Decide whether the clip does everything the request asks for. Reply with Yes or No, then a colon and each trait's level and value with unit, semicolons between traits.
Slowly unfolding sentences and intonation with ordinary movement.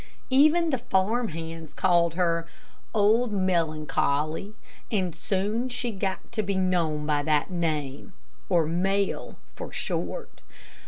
Yes: slow, 120 wpm; average, 4.7 semitones